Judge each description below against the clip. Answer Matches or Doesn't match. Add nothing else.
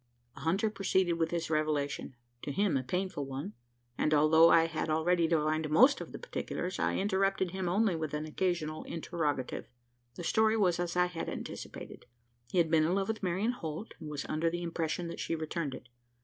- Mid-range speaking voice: Matches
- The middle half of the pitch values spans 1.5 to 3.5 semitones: Matches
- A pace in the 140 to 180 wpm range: Doesn't match